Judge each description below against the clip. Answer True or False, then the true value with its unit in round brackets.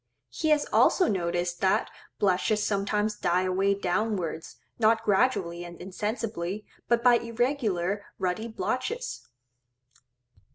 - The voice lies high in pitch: True (205 Hz)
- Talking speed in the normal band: False (110 wpm)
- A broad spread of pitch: False (4.1 semitones)